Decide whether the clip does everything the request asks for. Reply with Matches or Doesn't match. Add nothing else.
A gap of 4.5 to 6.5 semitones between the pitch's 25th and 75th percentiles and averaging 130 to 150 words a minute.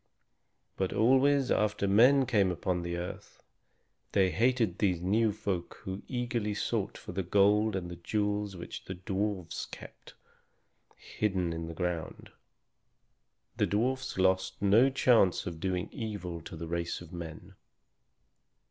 Doesn't match